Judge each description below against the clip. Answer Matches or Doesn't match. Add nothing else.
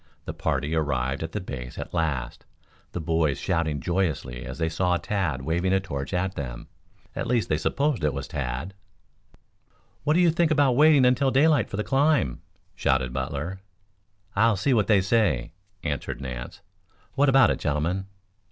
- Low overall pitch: Matches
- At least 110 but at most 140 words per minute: Doesn't match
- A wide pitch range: Matches